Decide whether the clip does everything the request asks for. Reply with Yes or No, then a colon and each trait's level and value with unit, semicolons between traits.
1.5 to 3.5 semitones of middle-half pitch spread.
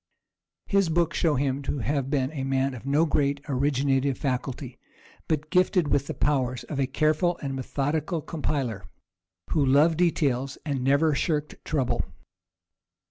Yes: narrow, 2.5 semitones